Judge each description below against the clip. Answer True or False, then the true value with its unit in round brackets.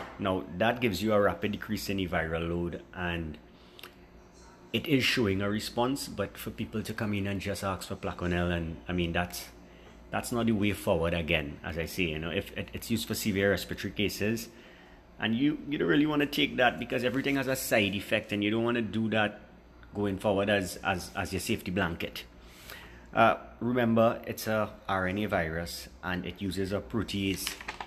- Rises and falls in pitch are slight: False (4.0 semitones)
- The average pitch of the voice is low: True (100 Hz)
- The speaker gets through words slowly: False (200 wpm)